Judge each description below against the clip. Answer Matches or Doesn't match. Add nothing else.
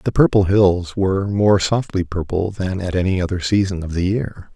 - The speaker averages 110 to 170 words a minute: Doesn't match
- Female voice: Doesn't match